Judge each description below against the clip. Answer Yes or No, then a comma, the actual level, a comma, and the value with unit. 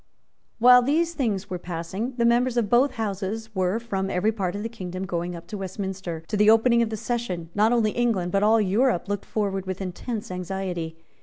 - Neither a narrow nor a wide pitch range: Yes, average, 4.0 semitones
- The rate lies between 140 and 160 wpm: No, fast, 205 wpm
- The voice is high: Yes, high, 205 Hz